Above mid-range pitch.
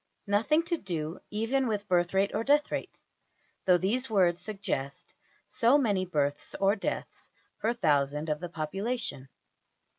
Yes: high, 195 Hz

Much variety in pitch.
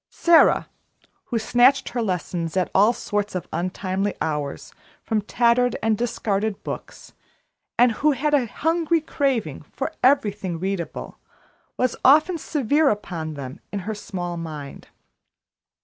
Yes: wide, 6.2 semitones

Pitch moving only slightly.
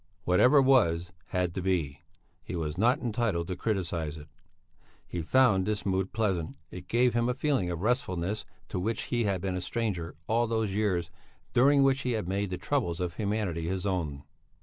No: average, 4.9 semitones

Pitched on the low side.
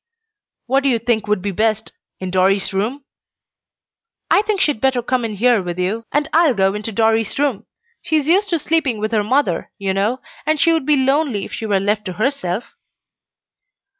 No: high, 225 Hz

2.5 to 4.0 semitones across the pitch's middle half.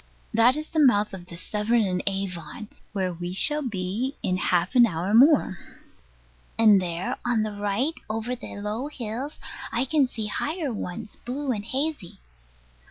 No: average, 5.1 semitones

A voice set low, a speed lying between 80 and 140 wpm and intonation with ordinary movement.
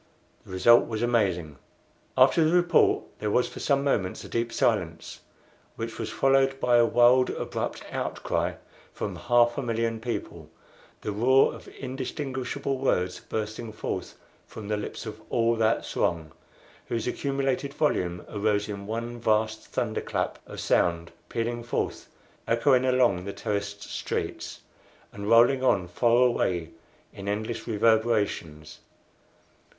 Yes: low, 115 Hz; slow, 135 wpm; average, 3.5 semitones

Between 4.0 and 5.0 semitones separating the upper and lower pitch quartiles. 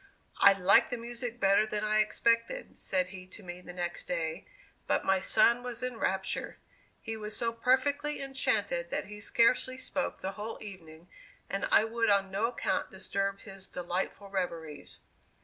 No: average, 3.6 semitones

